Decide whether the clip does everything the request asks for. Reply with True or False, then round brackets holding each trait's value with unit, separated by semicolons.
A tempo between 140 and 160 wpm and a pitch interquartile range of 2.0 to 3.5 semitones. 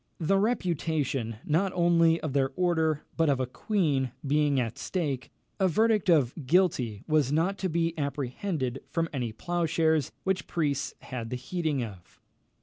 False (150 wpm; 4.6 semitones)